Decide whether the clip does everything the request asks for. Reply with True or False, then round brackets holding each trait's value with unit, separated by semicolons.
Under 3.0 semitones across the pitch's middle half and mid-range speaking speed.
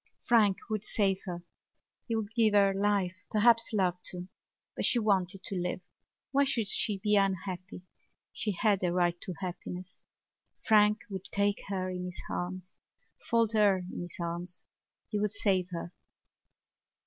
True (2.6 semitones; 155 wpm)